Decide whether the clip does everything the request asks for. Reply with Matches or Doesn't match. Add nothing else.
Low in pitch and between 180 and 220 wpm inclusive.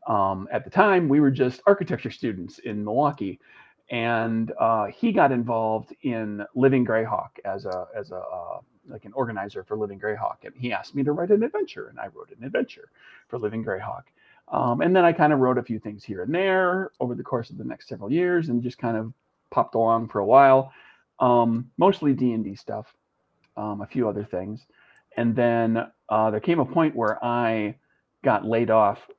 Matches